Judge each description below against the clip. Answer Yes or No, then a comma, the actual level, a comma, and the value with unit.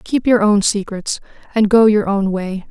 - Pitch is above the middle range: Yes, high, 205 Hz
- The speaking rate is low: No, average, 200 wpm